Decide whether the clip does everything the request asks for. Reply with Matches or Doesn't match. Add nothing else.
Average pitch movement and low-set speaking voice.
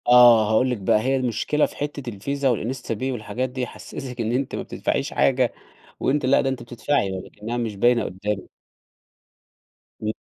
Matches